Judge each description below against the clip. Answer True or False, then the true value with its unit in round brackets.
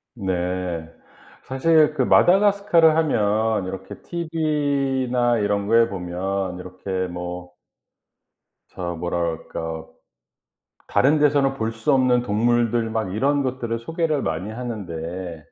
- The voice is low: True (115 Hz)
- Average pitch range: False (7.0 semitones)